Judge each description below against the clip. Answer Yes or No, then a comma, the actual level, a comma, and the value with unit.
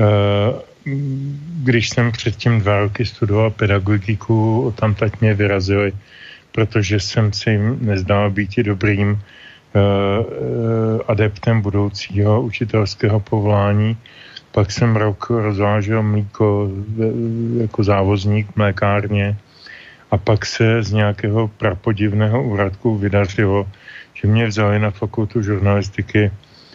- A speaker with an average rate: No, slow, 100 wpm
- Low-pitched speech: Yes, low, 105 Hz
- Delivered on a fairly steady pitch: Yes, narrow, 1.8 semitones